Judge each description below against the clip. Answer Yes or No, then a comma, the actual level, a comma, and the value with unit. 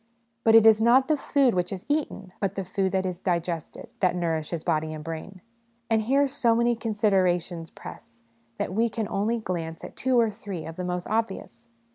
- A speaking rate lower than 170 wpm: No, average, 195 wpm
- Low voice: No, high, 190 Hz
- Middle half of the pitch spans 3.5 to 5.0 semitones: Yes, average, 4.7 semitones